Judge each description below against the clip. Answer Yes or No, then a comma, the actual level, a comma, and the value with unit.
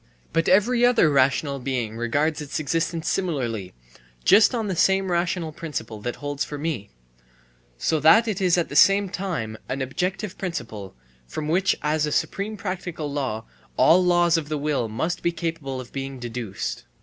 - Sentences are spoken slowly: No, average, 175 wpm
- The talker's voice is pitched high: No, medium, 155 Hz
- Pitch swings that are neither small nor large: No, wide, 5.8 semitones